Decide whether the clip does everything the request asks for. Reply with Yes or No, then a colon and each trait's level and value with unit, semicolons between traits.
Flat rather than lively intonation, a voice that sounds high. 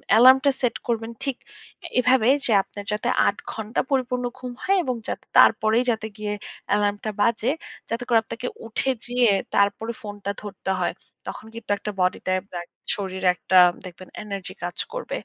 No: average, 3.4 semitones; high, 220 Hz